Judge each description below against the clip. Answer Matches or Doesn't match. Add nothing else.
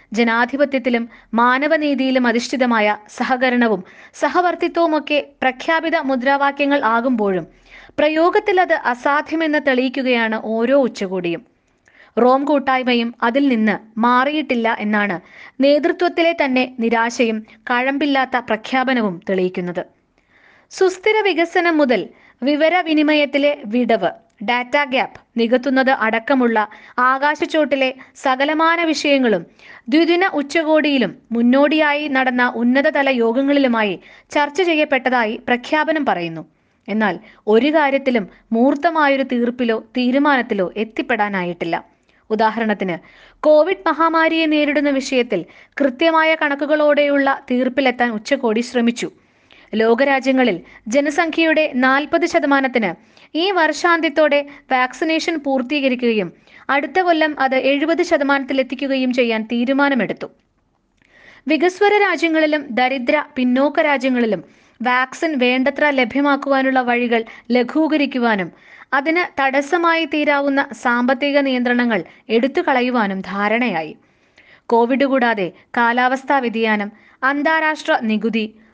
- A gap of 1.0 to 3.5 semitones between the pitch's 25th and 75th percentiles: Doesn't match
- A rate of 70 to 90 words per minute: Matches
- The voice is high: Matches